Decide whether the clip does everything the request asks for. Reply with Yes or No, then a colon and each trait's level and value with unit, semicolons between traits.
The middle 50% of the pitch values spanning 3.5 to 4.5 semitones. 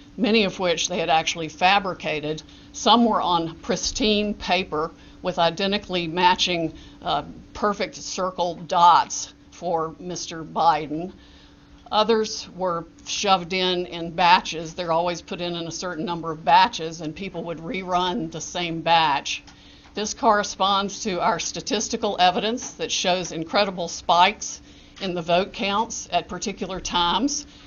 No: average, 3.1 semitones